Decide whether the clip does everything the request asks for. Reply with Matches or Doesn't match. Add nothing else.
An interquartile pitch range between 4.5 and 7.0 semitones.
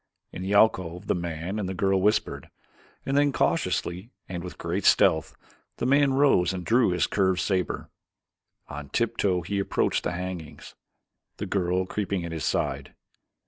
Doesn't match